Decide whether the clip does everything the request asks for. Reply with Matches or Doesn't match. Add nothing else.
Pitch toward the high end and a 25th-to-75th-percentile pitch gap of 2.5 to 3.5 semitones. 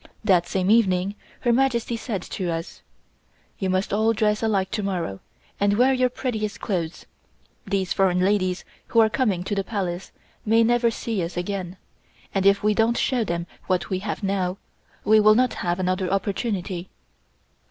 Matches